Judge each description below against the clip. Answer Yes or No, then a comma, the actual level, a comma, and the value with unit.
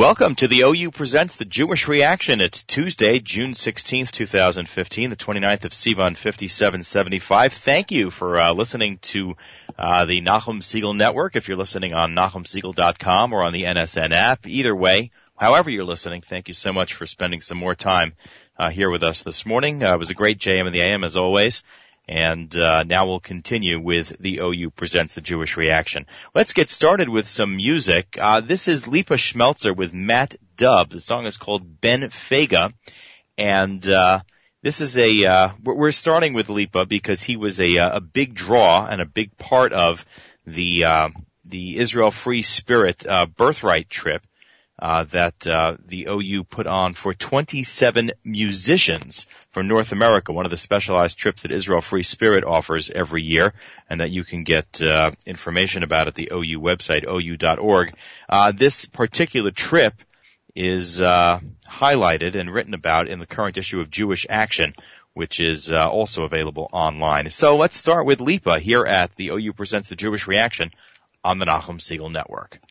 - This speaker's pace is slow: No, average, 175 wpm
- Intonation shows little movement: No, average, 4.0 semitones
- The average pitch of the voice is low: Yes, very low, 95 Hz